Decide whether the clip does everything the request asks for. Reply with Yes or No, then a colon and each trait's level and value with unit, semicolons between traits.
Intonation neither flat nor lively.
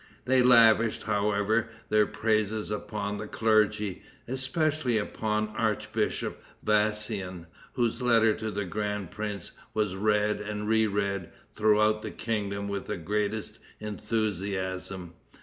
No: narrow, 1.5 semitones